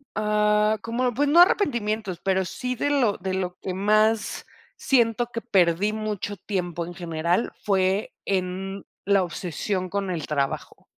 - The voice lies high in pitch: Yes, high, 200 Hz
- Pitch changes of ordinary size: Yes, average, 3.1 semitones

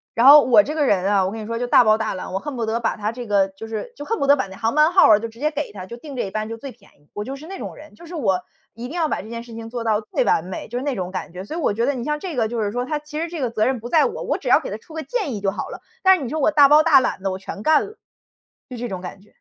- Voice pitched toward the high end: Yes, high, 240 Hz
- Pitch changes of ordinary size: No, wide, 5.9 semitones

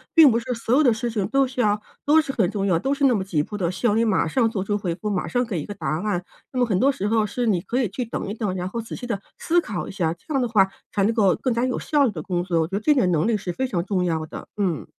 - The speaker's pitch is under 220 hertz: Yes, high, 210 Hz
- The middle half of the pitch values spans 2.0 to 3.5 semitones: No, average, 5.0 semitones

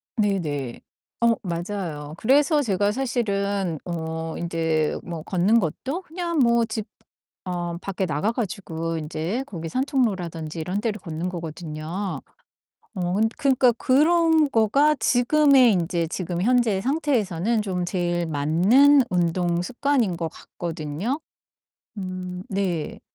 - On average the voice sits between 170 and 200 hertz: Yes, high, 190 Hz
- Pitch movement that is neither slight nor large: No, wide, 6.2 semitones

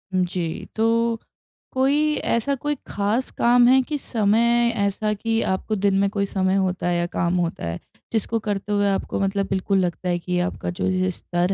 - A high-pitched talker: Yes, high, 200 Hz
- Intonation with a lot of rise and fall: No, average, 3.8 semitones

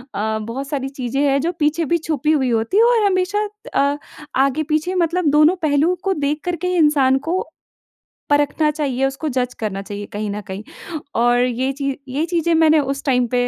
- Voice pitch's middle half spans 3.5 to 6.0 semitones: Yes, average, 4.0 semitones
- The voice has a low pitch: No, very high, 285 Hz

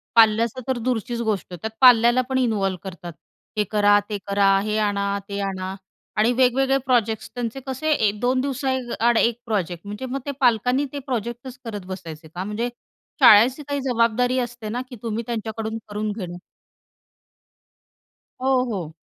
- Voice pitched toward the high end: Yes, high, 225 Hz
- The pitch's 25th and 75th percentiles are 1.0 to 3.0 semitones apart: No, average, 3.5 semitones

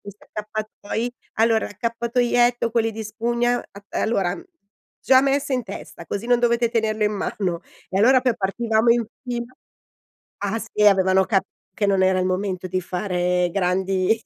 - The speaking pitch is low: No, high, 215 Hz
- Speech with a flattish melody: No, average, 3.7 semitones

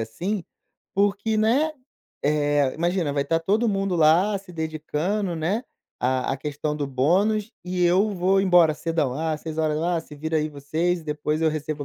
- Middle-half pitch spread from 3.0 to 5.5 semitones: Yes, average, 4.3 semitones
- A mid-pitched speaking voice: Yes, medium, 165 Hz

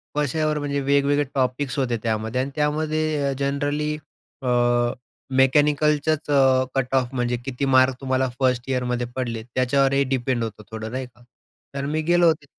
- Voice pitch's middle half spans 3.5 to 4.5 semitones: No, narrow, 2.6 semitones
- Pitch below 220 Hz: Yes, low, 135 Hz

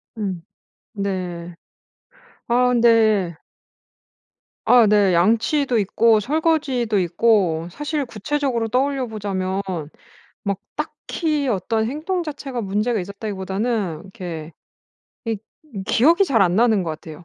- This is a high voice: Yes, high, 220 Hz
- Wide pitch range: No, average, 4.8 semitones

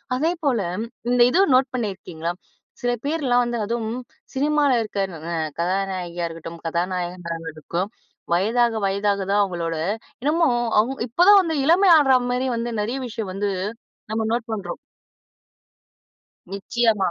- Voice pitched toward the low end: No, high, 220 Hz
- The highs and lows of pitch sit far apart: Yes, wide, 5.8 semitones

